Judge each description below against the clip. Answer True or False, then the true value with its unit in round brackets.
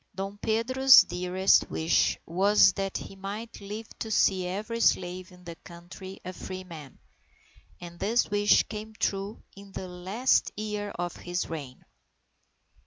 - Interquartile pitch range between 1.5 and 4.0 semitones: True (2.8 semitones)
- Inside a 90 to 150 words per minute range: True (145 wpm)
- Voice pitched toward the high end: True (195 Hz)